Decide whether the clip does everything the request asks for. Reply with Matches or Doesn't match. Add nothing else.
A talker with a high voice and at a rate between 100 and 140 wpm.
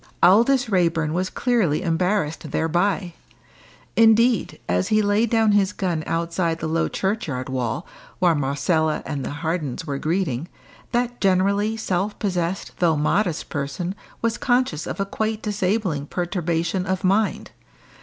Doesn't match